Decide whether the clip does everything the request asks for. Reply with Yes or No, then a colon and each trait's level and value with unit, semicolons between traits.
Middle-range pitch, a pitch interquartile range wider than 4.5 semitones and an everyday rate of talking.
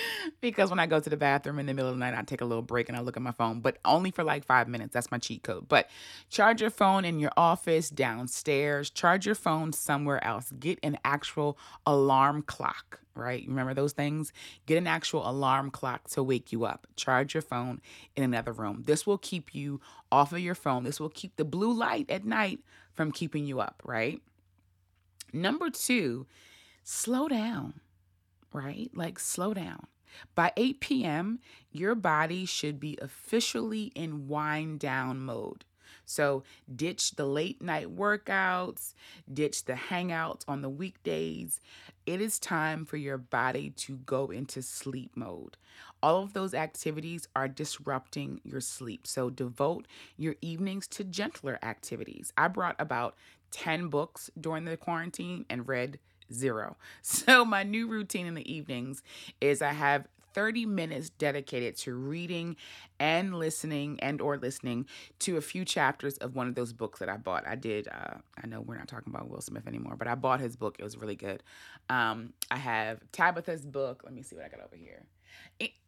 Yes: medium, 145 Hz; average, 5.1 semitones; average, 180 wpm